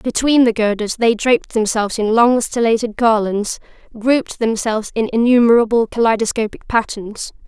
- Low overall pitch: No, high, 225 Hz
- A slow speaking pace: Yes, slow, 130 wpm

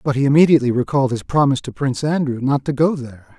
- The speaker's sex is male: Yes, male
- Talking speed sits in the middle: No, fast, 230 wpm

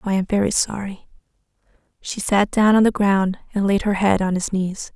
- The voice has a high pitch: Yes, high, 200 Hz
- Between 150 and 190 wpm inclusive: No, fast, 205 wpm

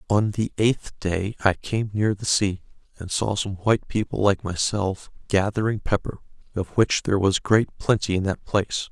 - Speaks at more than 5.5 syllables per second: No, 4.7 syllables/s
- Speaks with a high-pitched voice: No, low, 100 Hz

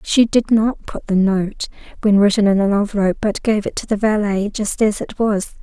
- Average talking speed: No, fast, 225 wpm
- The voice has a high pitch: Yes, high, 210 Hz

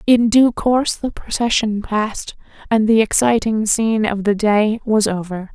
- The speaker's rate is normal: Yes, average, 160 wpm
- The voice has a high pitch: Yes, high, 220 Hz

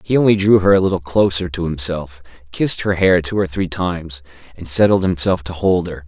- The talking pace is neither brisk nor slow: No, fast, 215 wpm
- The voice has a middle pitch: No, very low, 90 Hz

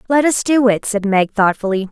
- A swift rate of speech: Yes, fast, 220 wpm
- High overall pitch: Yes, high, 220 Hz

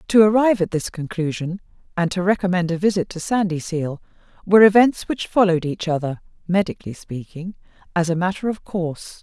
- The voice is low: No, medium, 180 Hz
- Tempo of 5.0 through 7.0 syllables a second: Yes, 5.5 syllables/s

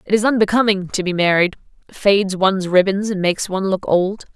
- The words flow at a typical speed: Yes, average, 180 wpm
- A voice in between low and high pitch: No, high, 195 Hz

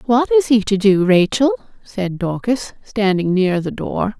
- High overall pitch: Yes, high, 215 Hz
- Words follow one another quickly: No, average, 170 wpm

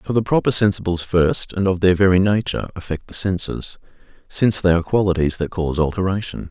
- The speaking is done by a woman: No, male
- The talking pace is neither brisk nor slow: Yes, average, 185 wpm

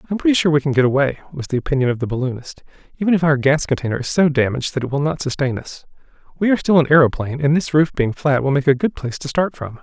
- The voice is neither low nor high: Yes, medium, 145 Hz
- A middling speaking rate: No, fast, 280 wpm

